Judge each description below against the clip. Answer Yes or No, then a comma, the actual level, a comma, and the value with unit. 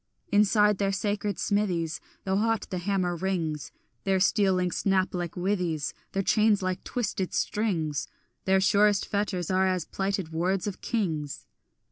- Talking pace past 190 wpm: No, average, 145 wpm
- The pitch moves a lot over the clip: No, narrow, 2.4 semitones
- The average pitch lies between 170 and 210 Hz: Yes, high, 190 Hz